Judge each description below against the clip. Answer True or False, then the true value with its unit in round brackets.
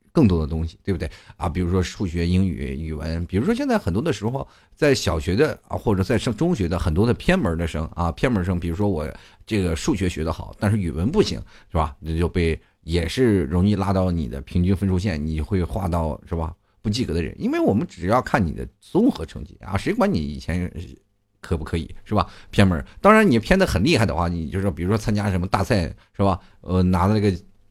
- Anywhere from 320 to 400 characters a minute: True (330 characters per minute)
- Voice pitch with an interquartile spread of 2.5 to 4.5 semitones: True (3.3 semitones)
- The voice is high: False (95 Hz)